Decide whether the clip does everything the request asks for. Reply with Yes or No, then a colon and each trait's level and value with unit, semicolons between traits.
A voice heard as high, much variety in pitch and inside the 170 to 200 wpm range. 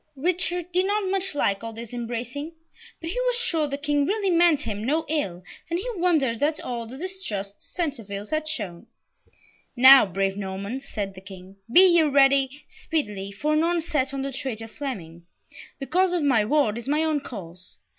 Yes: very high, 275 Hz; wide, 7.4 semitones; average, 185 wpm